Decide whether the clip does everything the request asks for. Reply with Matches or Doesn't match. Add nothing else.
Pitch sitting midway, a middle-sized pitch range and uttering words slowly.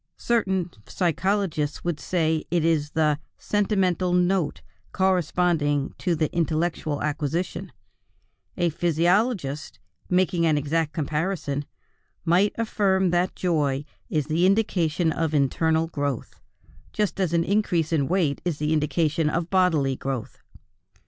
Matches